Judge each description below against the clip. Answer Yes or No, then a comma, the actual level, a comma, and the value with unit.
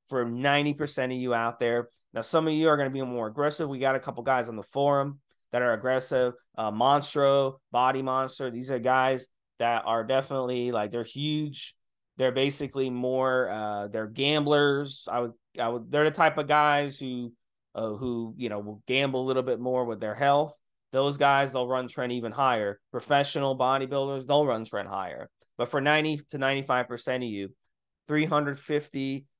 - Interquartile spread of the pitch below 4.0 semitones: Yes, average, 2.7 semitones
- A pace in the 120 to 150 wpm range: No, average, 185 wpm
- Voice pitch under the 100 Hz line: No, low, 130 Hz